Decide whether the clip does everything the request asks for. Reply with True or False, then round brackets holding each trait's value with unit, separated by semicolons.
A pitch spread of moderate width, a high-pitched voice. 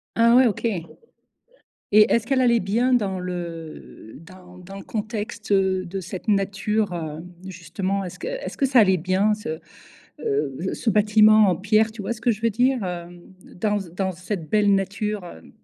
True (3.1 semitones; 200 Hz)